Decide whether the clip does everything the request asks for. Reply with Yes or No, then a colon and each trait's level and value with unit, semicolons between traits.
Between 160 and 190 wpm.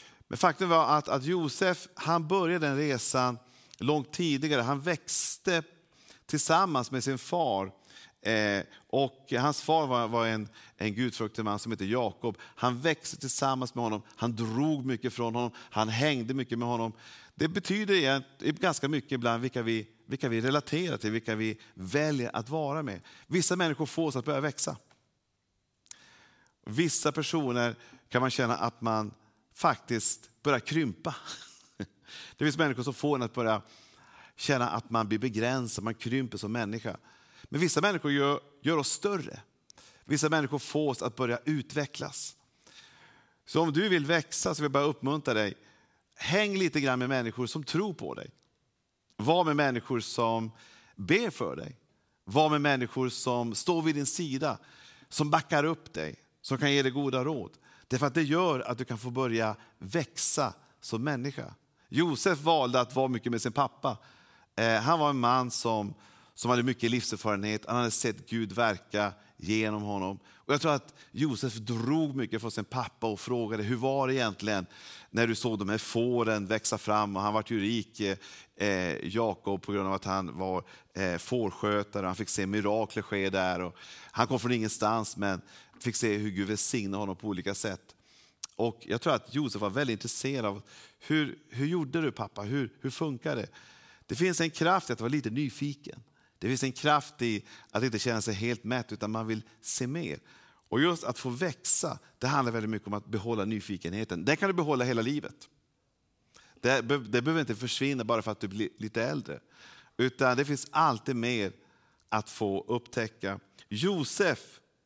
Yes: average, 175 wpm